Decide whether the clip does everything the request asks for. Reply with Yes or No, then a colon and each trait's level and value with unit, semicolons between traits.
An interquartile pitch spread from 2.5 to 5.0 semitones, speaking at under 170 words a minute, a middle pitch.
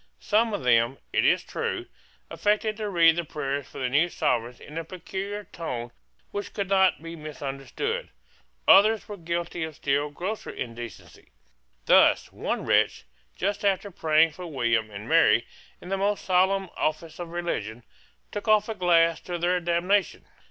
No: wide, 5.4 semitones; average, 160 wpm; medium, 170 Hz